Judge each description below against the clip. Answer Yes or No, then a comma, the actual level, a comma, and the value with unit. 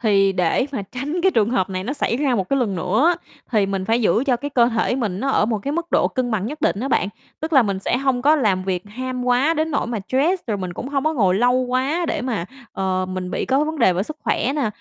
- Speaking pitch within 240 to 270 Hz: Yes, high, 245 Hz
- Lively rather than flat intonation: Yes, wide, 5.8 semitones